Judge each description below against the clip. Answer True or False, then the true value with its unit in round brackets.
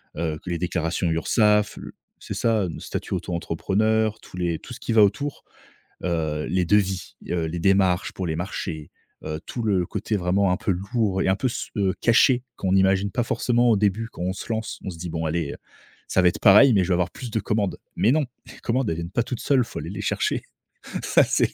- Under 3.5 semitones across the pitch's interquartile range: False (4.1 semitones)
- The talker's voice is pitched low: True (95 Hz)